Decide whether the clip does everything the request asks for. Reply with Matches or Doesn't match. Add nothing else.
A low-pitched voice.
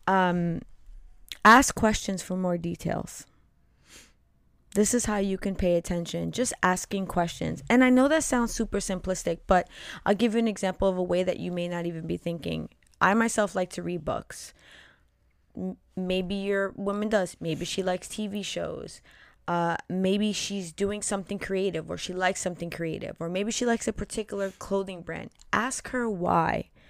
Doesn't match